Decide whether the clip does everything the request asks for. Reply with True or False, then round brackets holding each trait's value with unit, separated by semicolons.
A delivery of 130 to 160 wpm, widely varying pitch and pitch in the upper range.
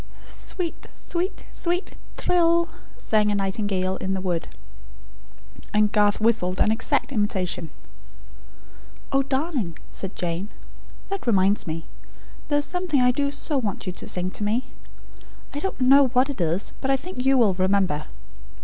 True (150 wpm; 6.9 semitones; 215 Hz)